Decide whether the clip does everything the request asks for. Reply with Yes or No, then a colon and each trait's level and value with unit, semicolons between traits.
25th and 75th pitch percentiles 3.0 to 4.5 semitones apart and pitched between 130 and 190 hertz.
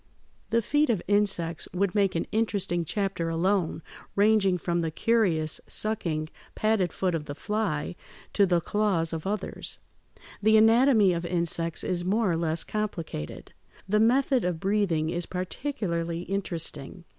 Yes: average, 4.1 semitones; medium, 185 Hz